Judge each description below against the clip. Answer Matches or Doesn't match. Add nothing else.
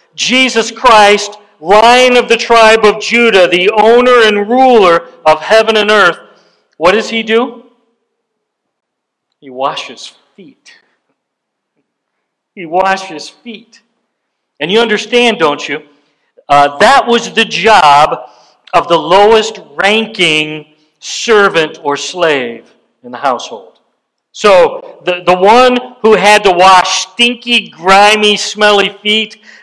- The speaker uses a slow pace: Matches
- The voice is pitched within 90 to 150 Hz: Doesn't match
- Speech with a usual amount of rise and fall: Matches